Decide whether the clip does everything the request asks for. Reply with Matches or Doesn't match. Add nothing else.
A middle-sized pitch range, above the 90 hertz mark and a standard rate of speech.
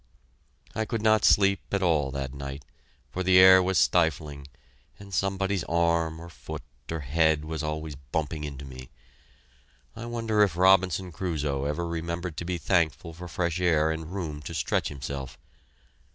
Doesn't match